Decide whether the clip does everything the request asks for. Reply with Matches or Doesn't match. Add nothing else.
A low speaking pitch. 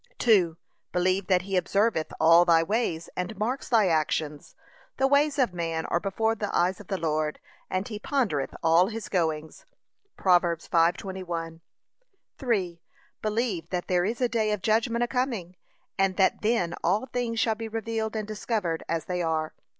Doesn't match